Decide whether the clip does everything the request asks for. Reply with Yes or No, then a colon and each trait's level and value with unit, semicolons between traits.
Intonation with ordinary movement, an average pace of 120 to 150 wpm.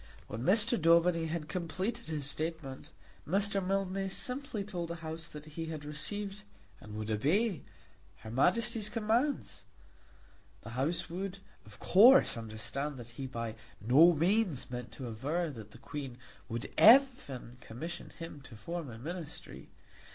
No: wide, 7.0 semitones; average, 145 wpm